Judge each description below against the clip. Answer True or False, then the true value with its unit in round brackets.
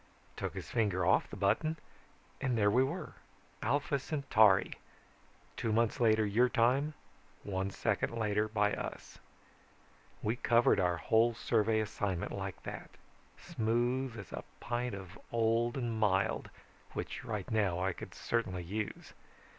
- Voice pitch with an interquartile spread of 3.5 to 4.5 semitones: False (2.9 semitones)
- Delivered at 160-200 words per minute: False (140 wpm)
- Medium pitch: False (110 Hz)